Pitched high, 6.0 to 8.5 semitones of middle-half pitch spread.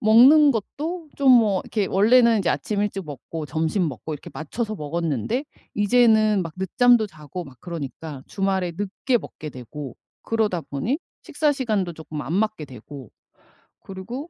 Yes: high, 195 Hz; wide, 6.9 semitones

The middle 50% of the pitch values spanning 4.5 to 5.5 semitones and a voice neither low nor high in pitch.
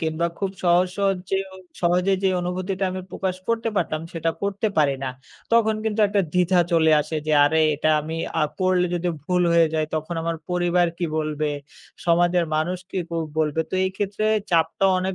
No: average, 2.7 semitones; medium, 175 Hz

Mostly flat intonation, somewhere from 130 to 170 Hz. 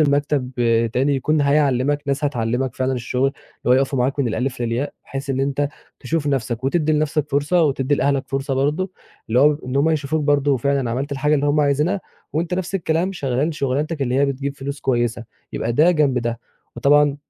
Yes: narrow, 2.2 semitones; medium, 140 Hz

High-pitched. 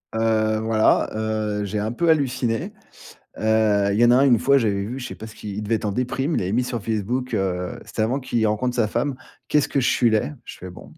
No: low, 110 Hz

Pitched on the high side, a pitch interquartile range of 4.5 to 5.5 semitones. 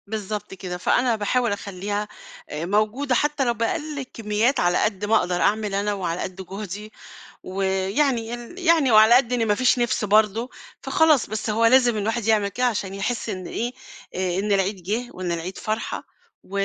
No: high, 215 Hz; average, 3.6 semitones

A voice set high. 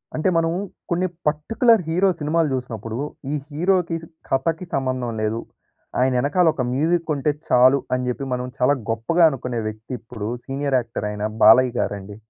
No: low, 135 Hz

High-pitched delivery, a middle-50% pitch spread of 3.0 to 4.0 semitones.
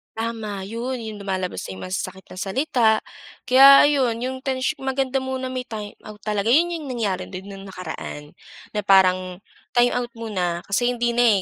No: high, 225 Hz; average, 5.0 semitones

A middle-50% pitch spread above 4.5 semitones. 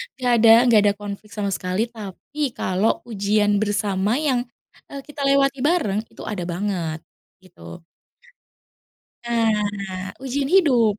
No: average, 3.8 semitones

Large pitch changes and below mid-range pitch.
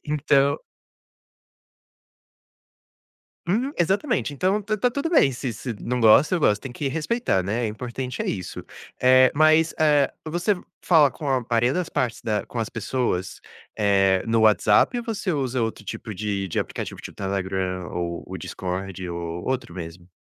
Yes: wide, 8.0 semitones; low, 125 Hz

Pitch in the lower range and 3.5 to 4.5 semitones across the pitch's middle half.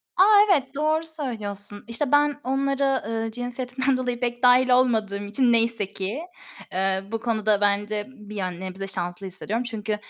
No: high, 230 Hz; average, 4.1 semitones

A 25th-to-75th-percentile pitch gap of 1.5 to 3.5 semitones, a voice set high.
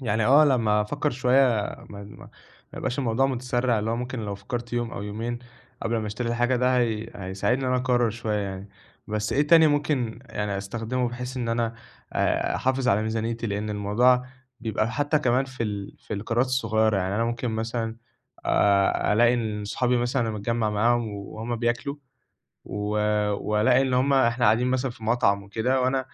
No: average, 3.0 semitones; low, 115 Hz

